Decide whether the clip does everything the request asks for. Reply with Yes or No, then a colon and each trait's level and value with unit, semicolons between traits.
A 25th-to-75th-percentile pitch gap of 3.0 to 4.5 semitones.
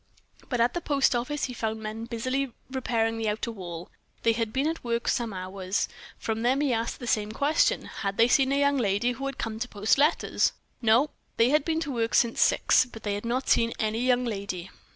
Yes: average, 3.3 semitones